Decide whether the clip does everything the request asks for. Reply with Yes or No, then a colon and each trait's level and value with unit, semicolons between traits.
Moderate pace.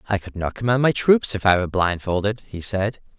No: fast, 225 wpm